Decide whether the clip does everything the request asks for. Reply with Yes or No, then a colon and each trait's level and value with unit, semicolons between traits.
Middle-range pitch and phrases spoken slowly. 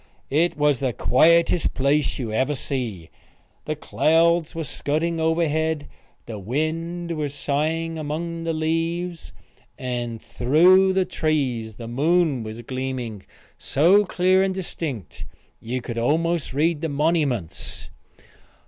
Yes: medium, 155 Hz; slow, 120 wpm